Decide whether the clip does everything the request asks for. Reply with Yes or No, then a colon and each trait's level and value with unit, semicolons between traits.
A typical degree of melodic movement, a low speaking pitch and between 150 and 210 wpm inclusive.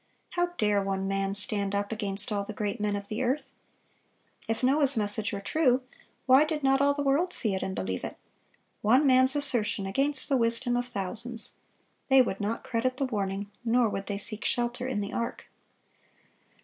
No: average, 4.4 semitones; high, 230 Hz; average, 190 wpm